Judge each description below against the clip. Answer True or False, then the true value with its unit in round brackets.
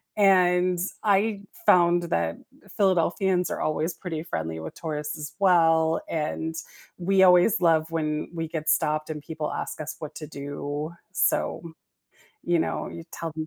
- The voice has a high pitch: False (165 Hz)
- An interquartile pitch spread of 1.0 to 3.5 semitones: True (2.7 semitones)